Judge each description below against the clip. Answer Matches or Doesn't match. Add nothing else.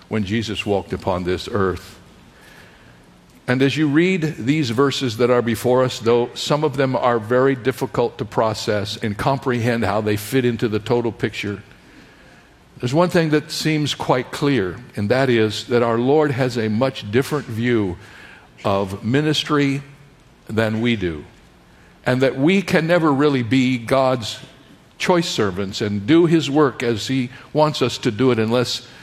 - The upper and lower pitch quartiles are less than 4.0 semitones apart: Doesn't match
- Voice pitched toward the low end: Matches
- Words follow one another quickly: Doesn't match